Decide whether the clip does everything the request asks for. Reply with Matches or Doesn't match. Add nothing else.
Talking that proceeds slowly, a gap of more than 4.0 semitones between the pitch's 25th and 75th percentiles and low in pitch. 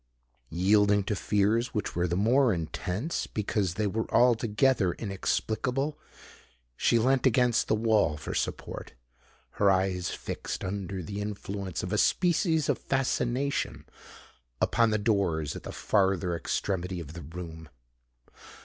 Matches